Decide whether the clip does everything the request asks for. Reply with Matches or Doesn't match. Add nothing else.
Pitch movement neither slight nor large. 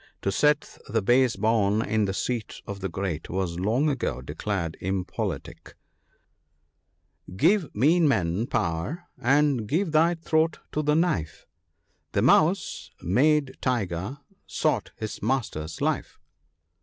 Doesn't match